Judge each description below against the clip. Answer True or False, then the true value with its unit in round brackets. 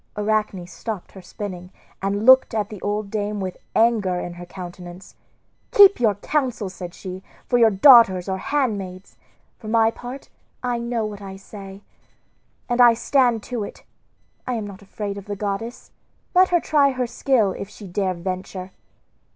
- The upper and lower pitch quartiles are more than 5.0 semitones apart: False (3.8 semitones)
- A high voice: True (205 Hz)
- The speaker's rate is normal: True (165 wpm)